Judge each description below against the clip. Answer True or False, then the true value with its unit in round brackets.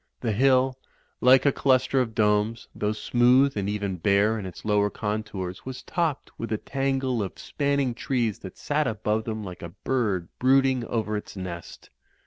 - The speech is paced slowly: False (170 wpm)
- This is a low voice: True (110 Hz)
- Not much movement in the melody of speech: False (4.1 semitones)